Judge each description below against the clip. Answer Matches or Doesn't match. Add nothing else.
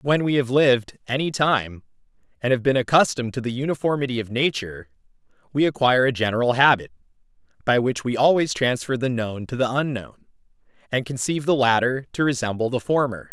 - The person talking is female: Doesn't match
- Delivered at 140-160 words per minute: Doesn't match